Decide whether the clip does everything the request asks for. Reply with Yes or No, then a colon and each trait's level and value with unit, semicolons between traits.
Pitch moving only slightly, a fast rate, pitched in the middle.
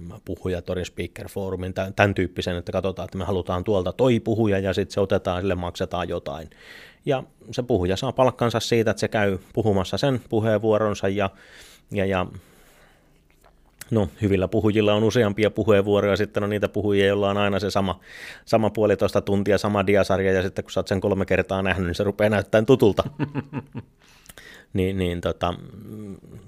No: narrow, 2.2 semitones; fast, 160 wpm; low, 100 Hz